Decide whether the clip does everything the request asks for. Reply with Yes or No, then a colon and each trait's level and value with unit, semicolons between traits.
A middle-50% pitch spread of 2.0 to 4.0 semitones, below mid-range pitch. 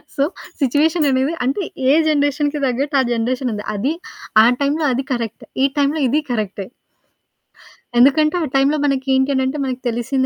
No: narrow, 2.5 semitones; very high, 270 Hz